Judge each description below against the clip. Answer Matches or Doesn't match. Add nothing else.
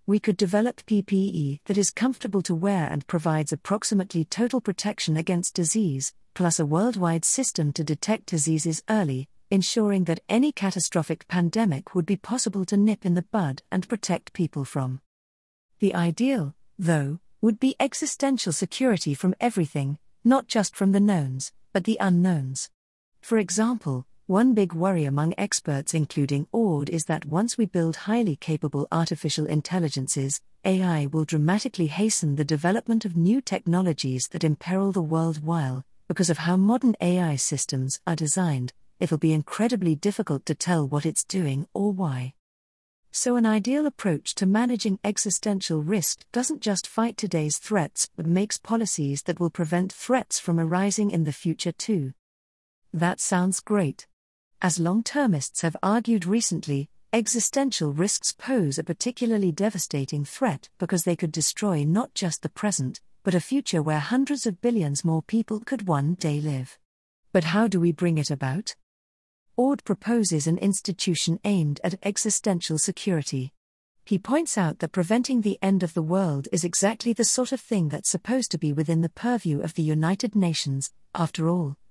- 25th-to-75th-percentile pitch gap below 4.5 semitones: Doesn't match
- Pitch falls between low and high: Matches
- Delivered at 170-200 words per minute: Doesn't match